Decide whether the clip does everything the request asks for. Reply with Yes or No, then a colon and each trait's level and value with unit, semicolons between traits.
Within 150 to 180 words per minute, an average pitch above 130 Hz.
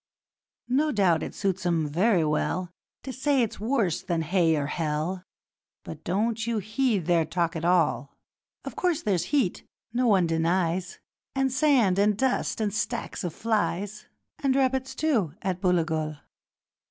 Yes: average, 155 wpm; high, 190 Hz